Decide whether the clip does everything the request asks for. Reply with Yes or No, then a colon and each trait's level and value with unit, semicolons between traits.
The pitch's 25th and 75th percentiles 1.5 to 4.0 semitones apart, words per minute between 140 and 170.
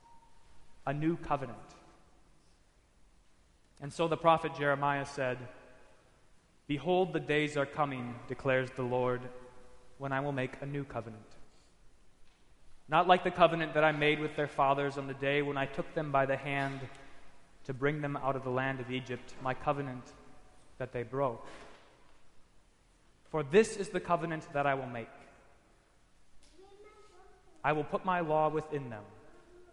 Yes: average, 3.4 semitones; average, 150 wpm